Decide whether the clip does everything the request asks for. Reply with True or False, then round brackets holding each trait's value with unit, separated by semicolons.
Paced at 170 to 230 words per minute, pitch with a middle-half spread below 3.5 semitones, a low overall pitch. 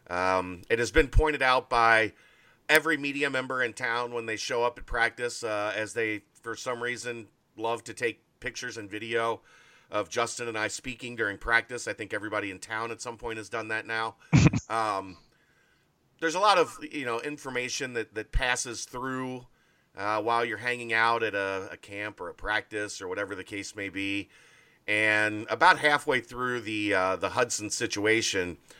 True (185 wpm; 2.8 semitones; 115 Hz)